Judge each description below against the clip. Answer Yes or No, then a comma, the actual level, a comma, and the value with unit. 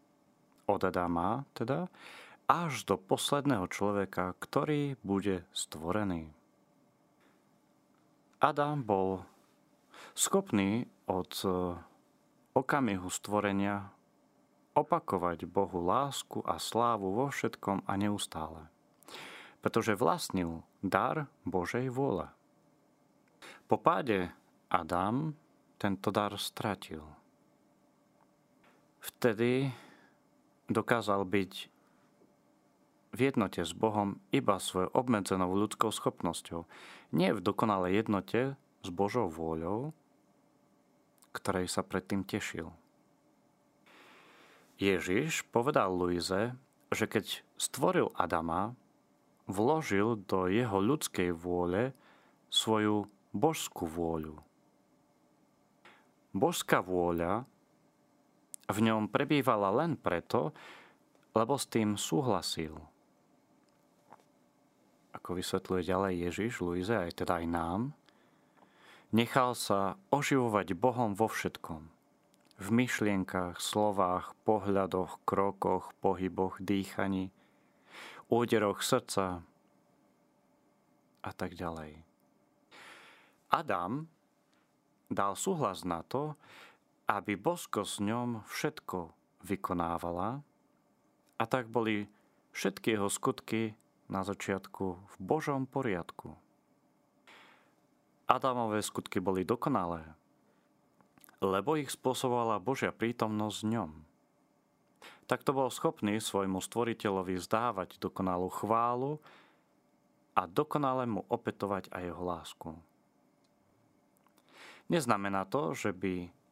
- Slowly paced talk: Yes, slow, 85 wpm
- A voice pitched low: Yes, low, 100 Hz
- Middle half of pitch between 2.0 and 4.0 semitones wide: No, average, 4.4 semitones